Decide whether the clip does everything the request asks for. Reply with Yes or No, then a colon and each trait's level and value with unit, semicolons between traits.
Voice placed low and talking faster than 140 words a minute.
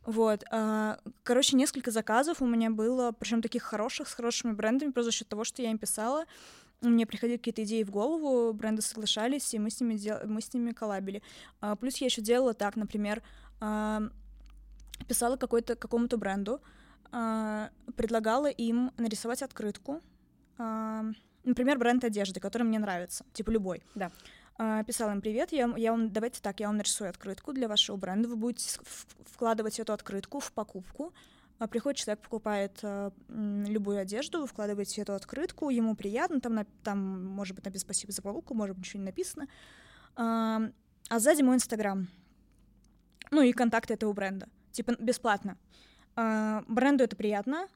No: high, 225 Hz; average, 155 wpm